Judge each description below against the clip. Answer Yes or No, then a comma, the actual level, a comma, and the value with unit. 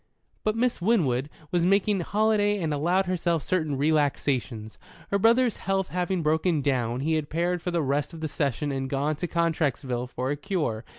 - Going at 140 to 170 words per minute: No, average, 180 wpm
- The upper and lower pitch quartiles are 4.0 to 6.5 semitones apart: Yes, average, 4.8 semitones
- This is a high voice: No, medium, 160 Hz